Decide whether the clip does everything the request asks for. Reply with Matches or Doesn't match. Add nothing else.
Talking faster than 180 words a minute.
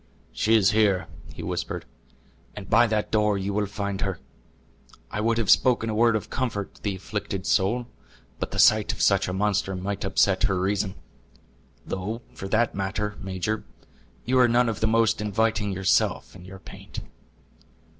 Doesn't match